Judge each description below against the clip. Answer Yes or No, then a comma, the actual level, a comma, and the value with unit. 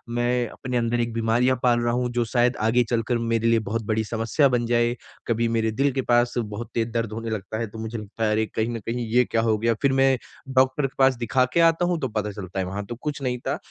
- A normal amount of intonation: No, narrow, 1.9 semitones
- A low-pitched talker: Yes, low, 120 Hz